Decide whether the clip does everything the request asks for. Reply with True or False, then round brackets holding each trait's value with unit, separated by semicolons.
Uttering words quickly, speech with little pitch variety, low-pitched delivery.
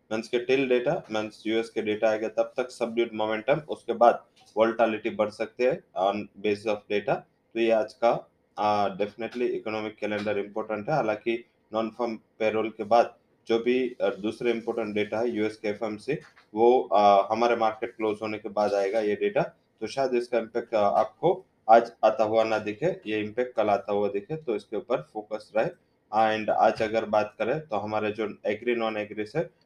False (180 wpm; 1.6 semitones; 110 Hz)